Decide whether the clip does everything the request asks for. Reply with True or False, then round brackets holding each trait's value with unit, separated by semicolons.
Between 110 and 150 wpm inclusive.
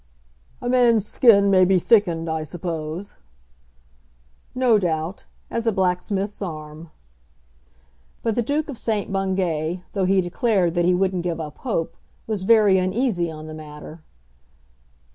True (140 wpm)